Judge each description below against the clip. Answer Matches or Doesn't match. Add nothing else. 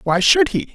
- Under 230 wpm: Doesn't match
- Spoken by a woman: Doesn't match